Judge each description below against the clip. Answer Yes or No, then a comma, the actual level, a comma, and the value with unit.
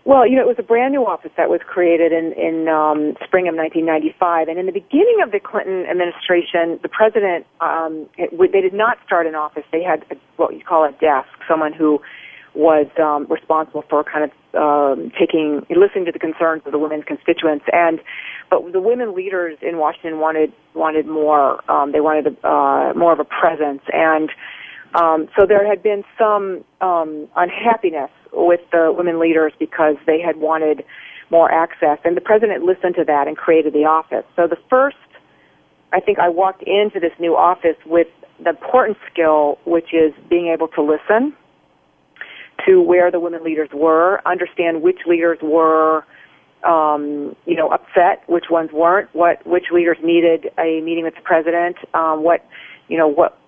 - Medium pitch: Yes, medium, 165 Hz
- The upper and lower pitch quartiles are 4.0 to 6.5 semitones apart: No, narrow, 2.5 semitones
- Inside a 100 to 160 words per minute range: No, average, 185 wpm